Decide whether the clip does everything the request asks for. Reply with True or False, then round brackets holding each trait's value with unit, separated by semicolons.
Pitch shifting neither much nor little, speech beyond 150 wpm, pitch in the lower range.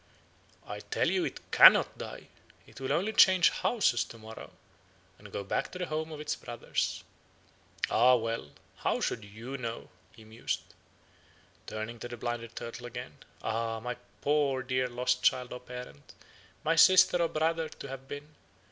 True (4.7 semitones; 165 wpm; 125 Hz)